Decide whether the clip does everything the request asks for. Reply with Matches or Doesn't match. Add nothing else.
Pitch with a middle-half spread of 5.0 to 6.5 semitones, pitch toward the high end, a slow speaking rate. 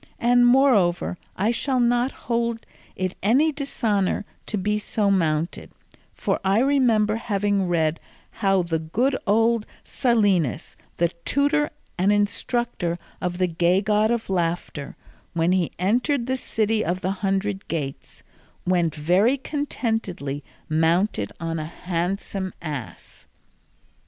Matches